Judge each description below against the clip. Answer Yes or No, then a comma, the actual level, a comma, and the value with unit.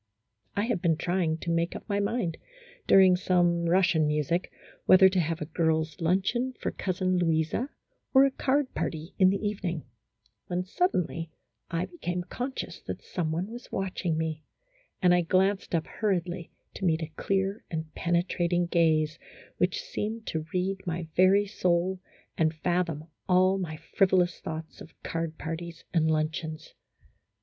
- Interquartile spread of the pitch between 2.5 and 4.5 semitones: Yes, average, 2.8 semitones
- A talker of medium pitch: Yes, medium, 175 Hz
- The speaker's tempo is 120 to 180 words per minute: Yes, average, 160 wpm